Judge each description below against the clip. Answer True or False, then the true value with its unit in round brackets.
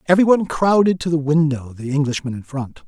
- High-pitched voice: False (150 Hz)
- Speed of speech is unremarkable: True (190 wpm)